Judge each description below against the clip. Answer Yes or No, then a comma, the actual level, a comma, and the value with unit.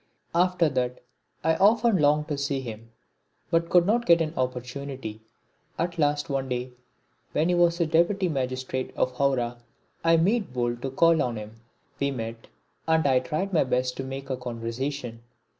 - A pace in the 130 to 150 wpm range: No, average, 160 wpm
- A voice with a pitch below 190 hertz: Yes, medium, 140 Hz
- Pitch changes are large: No, average, 4.9 semitones